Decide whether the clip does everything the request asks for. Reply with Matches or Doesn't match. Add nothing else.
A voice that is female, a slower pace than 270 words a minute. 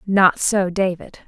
Matches